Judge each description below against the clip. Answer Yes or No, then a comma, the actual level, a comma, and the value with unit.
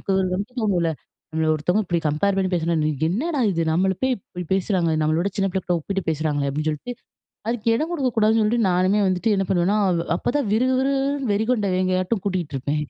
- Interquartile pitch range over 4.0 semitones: Yes, average, 4.7 semitones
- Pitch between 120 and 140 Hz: No, high, 190 Hz